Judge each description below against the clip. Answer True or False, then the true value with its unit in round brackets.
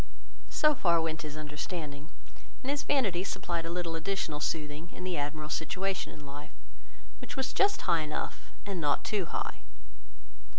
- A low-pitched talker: False (165 Hz)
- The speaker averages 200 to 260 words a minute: False (160 wpm)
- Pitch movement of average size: True (4.2 semitones)